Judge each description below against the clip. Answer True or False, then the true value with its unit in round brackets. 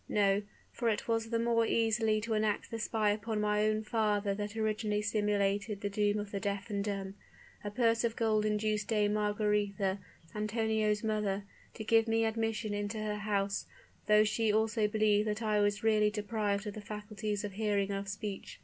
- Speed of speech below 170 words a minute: False (185 wpm)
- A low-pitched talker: False (210 Hz)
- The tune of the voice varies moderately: False (1.1 semitones)